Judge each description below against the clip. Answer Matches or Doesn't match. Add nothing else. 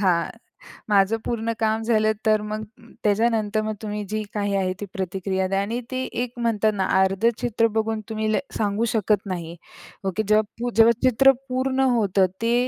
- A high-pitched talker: Matches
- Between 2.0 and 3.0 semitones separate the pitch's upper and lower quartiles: Matches